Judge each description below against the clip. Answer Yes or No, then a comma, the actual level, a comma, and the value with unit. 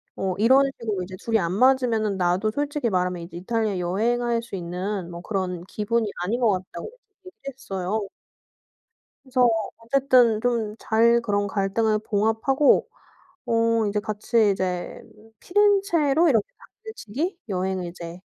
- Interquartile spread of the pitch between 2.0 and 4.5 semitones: Yes, average, 4.2 semitones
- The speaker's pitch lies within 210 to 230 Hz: Yes, high, 220 Hz